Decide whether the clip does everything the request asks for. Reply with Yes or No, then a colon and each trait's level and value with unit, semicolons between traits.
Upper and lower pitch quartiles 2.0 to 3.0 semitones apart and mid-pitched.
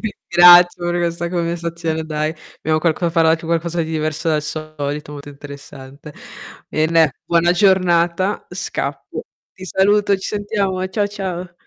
Yes: average, 2.7 semitones; medium, 170 Hz